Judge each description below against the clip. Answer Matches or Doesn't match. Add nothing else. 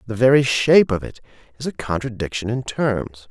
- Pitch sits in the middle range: Doesn't match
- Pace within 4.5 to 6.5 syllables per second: Matches